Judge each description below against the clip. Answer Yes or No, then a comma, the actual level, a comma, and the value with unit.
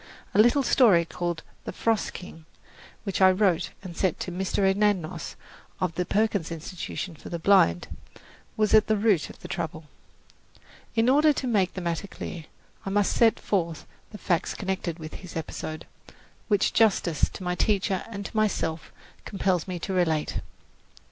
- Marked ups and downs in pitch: No, average, 3.6 semitones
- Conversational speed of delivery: Yes, average, 165 wpm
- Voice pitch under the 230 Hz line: Yes, high, 190 Hz